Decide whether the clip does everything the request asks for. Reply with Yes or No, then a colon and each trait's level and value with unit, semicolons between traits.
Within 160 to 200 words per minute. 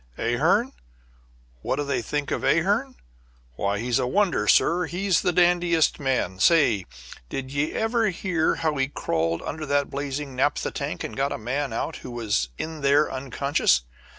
Yes: average, 165 wpm